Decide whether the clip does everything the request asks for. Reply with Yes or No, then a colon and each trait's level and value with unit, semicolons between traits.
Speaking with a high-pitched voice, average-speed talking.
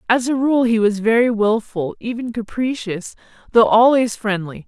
Yes: high, 225 Hz; average, 155 wpm